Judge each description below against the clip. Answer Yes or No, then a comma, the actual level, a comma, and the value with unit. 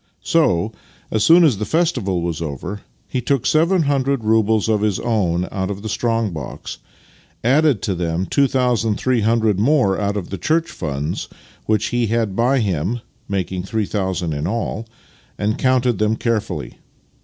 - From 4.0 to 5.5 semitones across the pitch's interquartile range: Yes, average, 4.7 semitones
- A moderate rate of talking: Yes, average, 170 wpm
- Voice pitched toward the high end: No, low, 110 Hz